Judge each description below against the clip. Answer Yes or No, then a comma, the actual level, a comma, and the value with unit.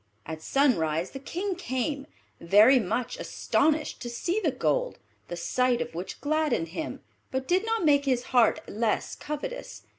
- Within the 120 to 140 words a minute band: No, average, 155 wpm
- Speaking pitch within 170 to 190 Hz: No, very high, 260 Hz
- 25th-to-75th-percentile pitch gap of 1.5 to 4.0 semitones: No, wide, 5.4 semitones